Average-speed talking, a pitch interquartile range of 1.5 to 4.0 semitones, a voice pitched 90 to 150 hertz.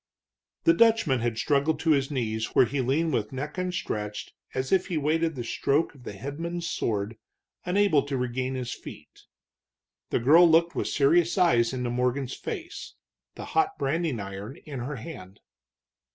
No: average, 165 wpm; wide, 5.5 semitones; medium, 140 Hz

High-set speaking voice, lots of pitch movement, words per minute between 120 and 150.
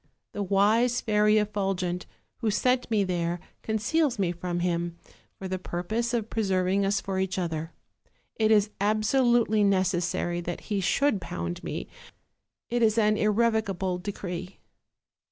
No: high, 200 Hz; average, 3.3 semitones; slow, 135 wpm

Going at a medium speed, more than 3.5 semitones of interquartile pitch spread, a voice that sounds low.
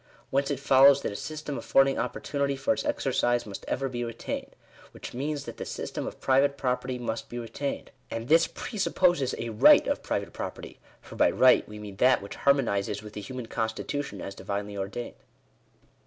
Yes: average, 180 wpm; average, 4.1 semitones; low, 125 Hz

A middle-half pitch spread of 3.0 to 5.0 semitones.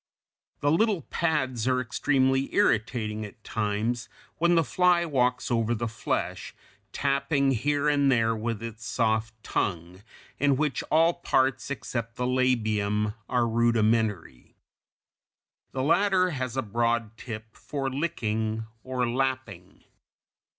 Yes: average, 3.9 semitones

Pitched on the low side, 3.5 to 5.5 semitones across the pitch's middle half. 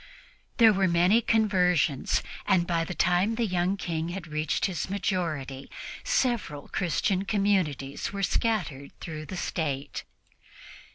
No: medium, 180 Hz; average, 4.1 semitones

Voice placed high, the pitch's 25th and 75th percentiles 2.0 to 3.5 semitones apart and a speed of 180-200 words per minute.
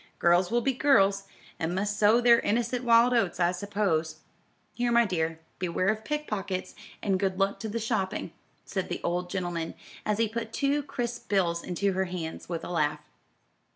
No: high, 195 Hz; average, 4.7 semitones; average, 185 wpm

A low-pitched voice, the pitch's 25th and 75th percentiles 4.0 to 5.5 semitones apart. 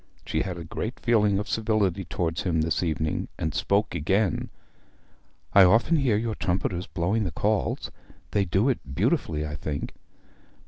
Yes: very low, 95 Hz; average, 4.6 semitones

